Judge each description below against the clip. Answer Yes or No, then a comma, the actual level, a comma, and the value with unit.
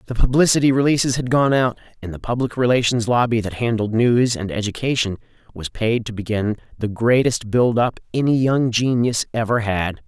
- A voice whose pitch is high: No, low, 115 Hz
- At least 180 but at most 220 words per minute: No, average, 165 wpm